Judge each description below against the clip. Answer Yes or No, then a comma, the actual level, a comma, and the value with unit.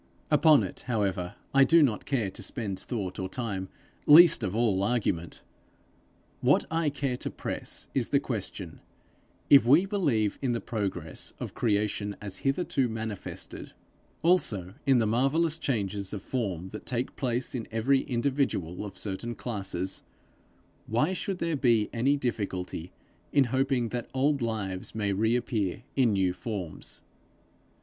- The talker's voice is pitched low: Yes, low, 115 Hz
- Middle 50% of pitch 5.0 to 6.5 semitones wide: Yes, wide, 5.4 semitones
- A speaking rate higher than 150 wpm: No, average, 145 wpm